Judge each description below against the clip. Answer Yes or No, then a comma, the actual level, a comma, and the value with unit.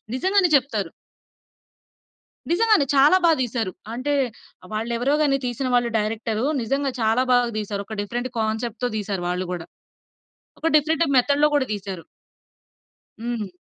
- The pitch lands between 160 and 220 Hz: No, high, 240 Hz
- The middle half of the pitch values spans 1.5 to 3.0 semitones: No, average, 4.6 semitones